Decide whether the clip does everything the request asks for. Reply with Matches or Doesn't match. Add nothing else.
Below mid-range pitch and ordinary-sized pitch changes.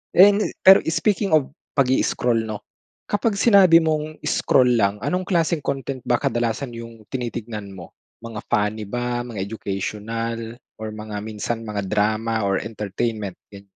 Matches